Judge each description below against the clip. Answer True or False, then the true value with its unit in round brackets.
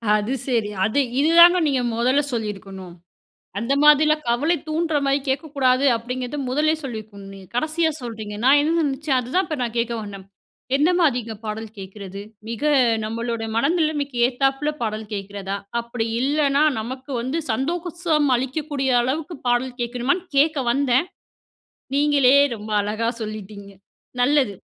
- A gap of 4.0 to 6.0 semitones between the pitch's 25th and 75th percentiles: True (5.1 semitones)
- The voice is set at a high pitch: True (255 Hz)